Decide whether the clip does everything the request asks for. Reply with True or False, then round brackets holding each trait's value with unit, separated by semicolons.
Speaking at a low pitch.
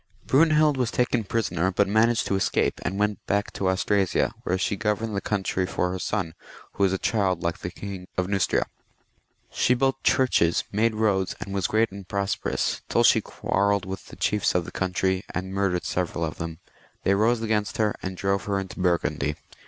True (100 Hz)